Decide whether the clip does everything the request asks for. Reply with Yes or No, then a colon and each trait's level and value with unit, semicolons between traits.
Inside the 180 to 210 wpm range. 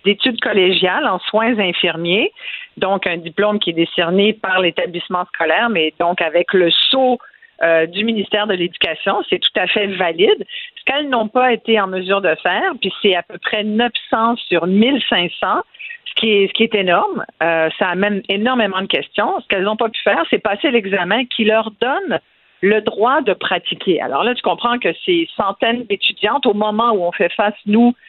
Yes: average, 190 wpm